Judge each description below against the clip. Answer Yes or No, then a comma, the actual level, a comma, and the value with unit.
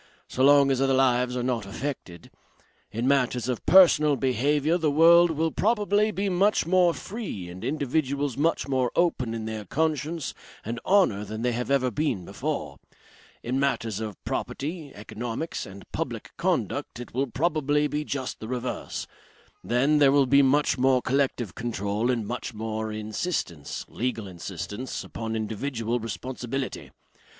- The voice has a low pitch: Yes, low, 130 Hz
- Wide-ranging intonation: No, average, 4.7 semitones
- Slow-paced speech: No, average, 150 wpm